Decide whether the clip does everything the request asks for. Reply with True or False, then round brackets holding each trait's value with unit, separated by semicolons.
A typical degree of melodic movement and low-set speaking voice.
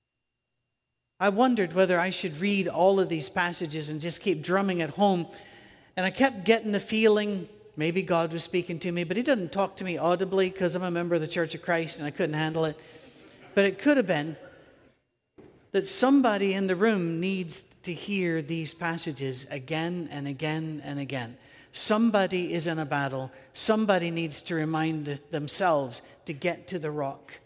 False (3.5 semitones; 170 Hz)